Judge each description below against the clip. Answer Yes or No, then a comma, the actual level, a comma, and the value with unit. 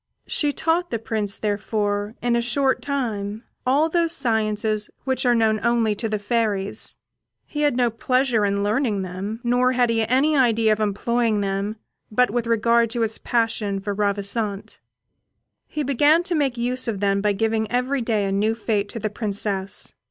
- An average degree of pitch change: Yes, average, 3.2 semitones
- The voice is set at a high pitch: Yes, high, 225 Hz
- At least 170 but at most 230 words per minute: Yes, average, 175 wpm